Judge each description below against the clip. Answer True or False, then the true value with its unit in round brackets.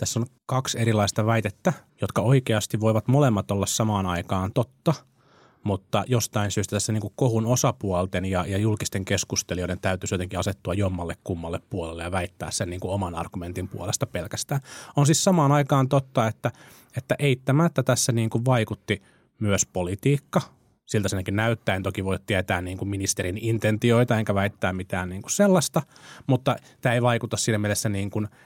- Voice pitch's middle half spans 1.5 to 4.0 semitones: False (4.8 semitones)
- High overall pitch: False (110 Hz)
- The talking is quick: True (160 wpm)